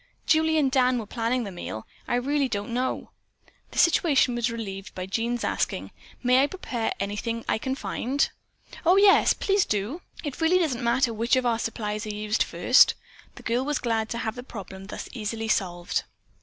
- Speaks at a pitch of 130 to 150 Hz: No, high, 235 Hz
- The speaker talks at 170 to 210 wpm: Yes, average, 185 wpm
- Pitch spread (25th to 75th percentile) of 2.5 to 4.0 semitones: Yes, average, 3.5 semitones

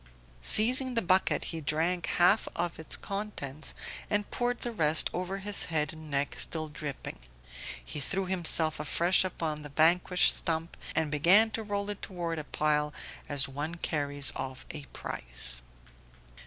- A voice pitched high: No, medium, 160 Hz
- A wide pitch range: No, average, 4.2 semitones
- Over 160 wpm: No, average, 150 wpm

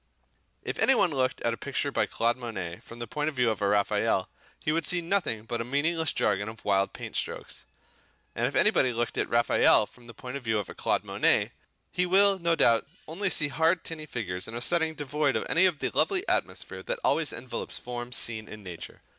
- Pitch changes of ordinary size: No, wide, 6.0 semitones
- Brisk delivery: Yes, fast, 220 wpm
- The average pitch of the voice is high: No, low, 130 Hz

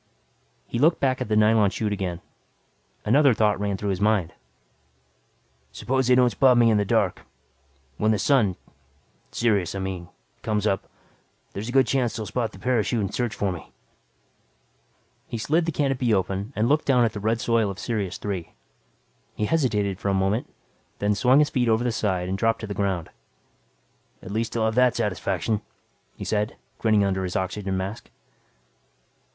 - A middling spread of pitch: Yes, average, 3.4 semitones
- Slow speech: No, average, 180 wpm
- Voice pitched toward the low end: Yes, low, 110 Hz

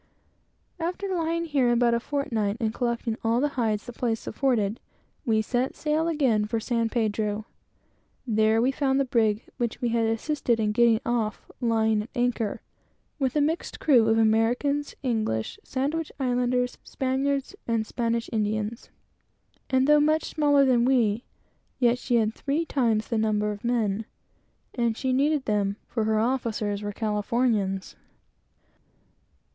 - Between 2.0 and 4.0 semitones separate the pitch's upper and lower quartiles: Yes, average, 3.5 semitones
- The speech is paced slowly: No, average, 150 wpm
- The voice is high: Yes, high, 235 Hz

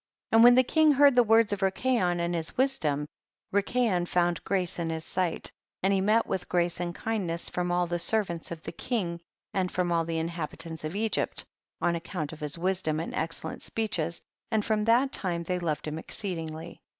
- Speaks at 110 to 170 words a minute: No, average, 200 wpm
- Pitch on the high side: No, medium, 175 Hz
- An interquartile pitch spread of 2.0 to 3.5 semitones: No, average, 4.4 semitones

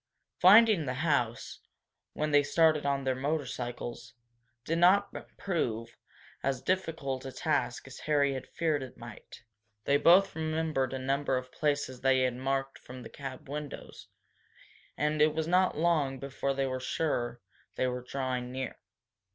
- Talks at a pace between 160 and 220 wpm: No, average, 150 wpm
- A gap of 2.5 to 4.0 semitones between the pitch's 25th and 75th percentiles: Yes, average, 3.3 semitones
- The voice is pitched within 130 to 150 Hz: Yes, medium, 140 Hz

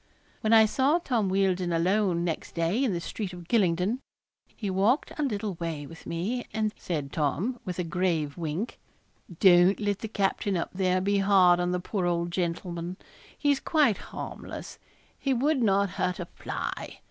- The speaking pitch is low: No, high, 190 Hz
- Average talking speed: Yes, average, 170 wpm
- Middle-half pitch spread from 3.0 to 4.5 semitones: Yes, average, 3.7 semitones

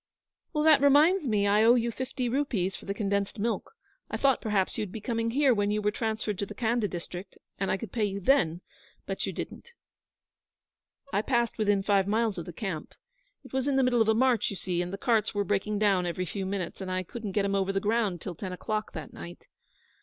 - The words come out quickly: Yes, fast, 230 wpm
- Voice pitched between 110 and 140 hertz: No, high, 210 Hz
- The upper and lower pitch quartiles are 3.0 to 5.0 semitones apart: Yes, average, 3.5 semitones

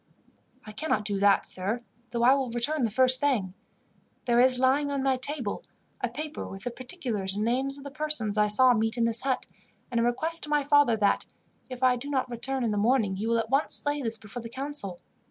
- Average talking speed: No, fast, 225 wpm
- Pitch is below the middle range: No, high, 245 Hz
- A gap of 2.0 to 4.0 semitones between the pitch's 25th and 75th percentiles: Yes, average, 3.7 semitones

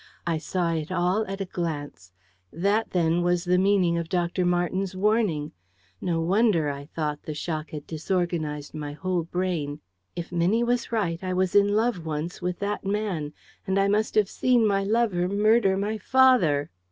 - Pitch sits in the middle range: Yes, medium, 180 Hz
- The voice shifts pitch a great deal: No, average, 3.6 semitones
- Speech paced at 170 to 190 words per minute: Yes, average, 175 wpm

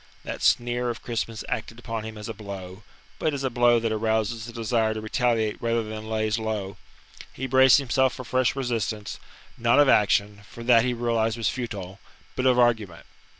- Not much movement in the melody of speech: Yes, narrow, 1.9 semitones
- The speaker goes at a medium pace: Yes, average, 190 wpm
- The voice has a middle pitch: No, low, 115 Hz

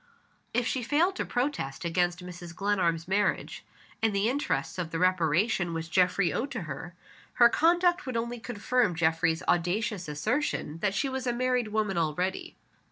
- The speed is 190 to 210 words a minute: No, average, 165 wpm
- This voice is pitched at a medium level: No, high, 195 Hz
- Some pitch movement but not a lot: No, wide, 6.1 semitones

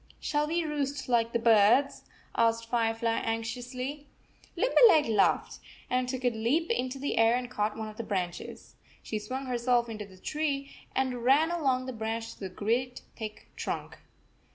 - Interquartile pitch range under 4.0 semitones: Yes, average, 3.3 semitones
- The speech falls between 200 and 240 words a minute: No, average, 165 wpm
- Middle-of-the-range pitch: No, high, 245 Hz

